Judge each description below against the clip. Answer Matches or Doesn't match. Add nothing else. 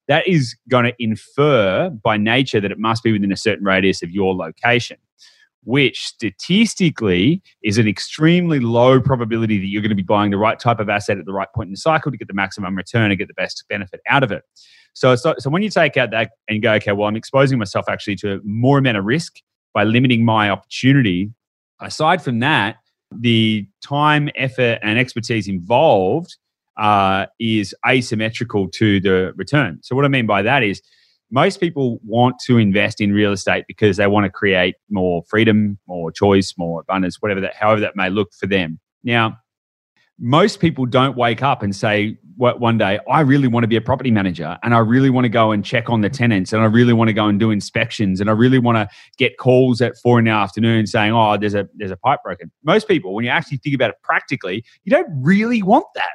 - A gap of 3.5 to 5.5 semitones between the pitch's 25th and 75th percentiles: Matches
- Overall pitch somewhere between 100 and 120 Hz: Matches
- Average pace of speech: Doesn't match